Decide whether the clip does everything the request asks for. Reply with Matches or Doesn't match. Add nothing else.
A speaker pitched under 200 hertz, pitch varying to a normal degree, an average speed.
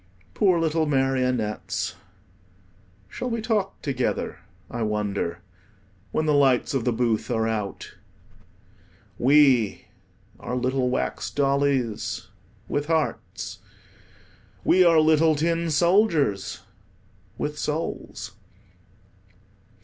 Doesn't match